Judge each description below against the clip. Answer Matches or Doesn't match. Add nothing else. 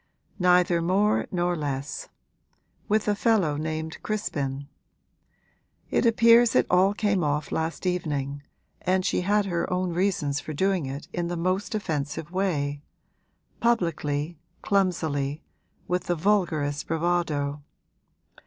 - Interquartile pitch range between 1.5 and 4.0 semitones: Doesn't match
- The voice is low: Doesn't match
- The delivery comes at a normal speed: Doesn't match